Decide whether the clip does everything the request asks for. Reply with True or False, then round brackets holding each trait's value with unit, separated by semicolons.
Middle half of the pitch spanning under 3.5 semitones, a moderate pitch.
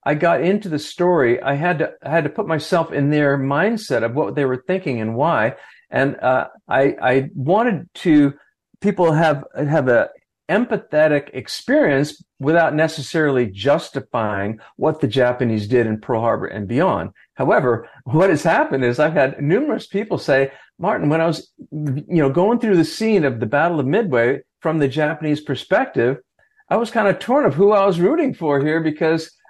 False (4.2 semitones; 155 Hz)